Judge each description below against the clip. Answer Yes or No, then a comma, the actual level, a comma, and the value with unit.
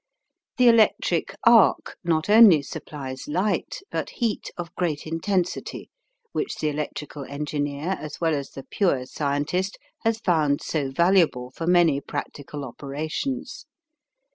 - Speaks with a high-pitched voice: No, medium, 160 Hz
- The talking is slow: Yes, slow, 125 wpm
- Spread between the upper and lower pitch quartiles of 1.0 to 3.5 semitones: No, average, 4.8 semitones